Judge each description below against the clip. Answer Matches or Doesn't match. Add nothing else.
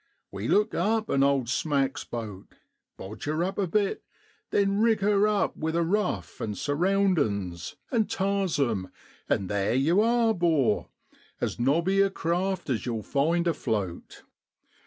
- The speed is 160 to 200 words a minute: Doesn't match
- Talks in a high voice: Doesn't match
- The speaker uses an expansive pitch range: Matches